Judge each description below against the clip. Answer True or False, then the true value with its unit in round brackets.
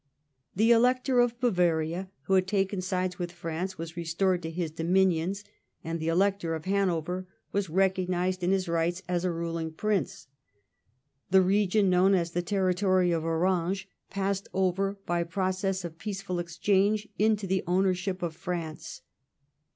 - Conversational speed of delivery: True (150 wpm)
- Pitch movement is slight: True (2.3 semitones)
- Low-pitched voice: False (185 Hz)